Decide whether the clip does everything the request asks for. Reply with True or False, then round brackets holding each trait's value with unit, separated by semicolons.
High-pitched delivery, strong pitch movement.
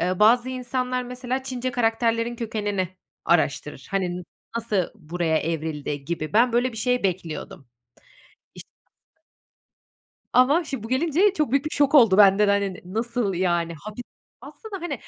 True (225 Hz; 5.8 semitones)